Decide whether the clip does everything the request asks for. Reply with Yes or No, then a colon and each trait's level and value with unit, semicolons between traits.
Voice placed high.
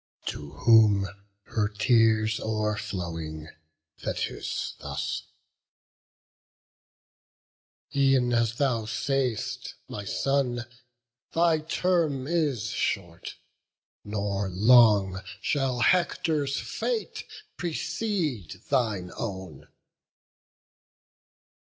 No: low, 115 Hz